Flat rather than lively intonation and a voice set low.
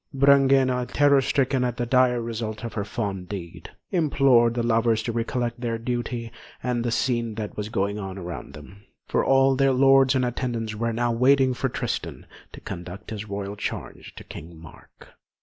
No: average, 3.2 semitones; low, 120 Hz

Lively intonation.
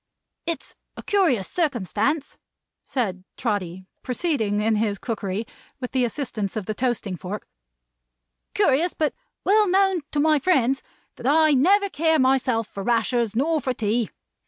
Yes: wide, 6.5 semitones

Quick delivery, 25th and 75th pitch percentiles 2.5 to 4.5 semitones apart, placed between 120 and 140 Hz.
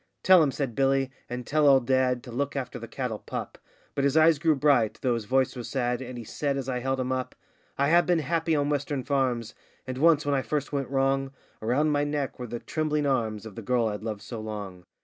Yes: fast, 240 wpm; average, 3.0 semitones; low, 135 Hz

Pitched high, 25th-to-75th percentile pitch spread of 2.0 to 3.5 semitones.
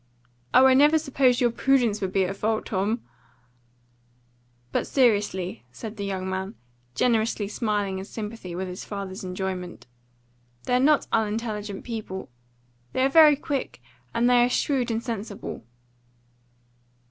No: high, 215 Hz; average, 4.4 semitones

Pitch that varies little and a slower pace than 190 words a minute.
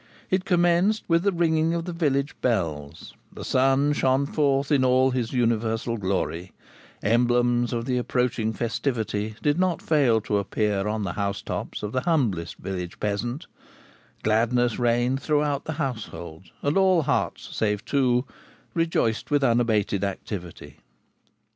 No: average, 5.3 semitones; average, 140 wpm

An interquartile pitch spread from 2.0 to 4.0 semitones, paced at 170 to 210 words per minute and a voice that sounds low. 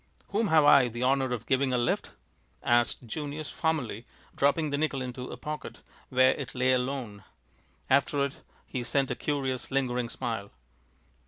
No: narrow, 2.5 semitones; average, 160 wpm; low, 130 Hz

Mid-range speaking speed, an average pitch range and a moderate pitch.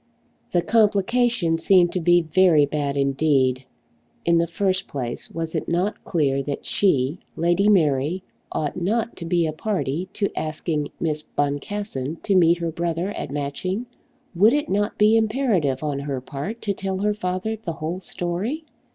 Yes: average, 160 wpm; average, 5.0 semitones; medium, 170 Hz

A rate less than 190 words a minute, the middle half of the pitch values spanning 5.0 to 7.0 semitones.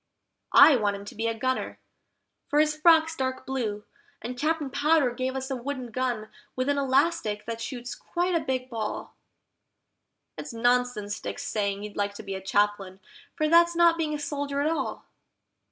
Yes: average, 180 wpm; wide, 5.4 semitones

